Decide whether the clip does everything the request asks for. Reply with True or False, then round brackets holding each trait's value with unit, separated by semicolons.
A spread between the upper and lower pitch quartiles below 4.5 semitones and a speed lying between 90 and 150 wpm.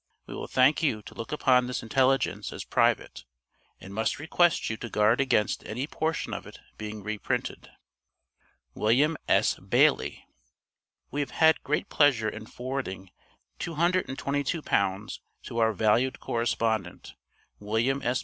False (4.8 semitones; 135 wpm)